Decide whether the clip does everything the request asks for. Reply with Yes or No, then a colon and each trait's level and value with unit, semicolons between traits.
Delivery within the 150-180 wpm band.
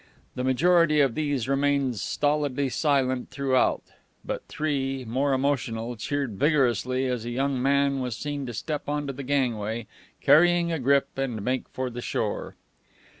Yes: average, 155 wpm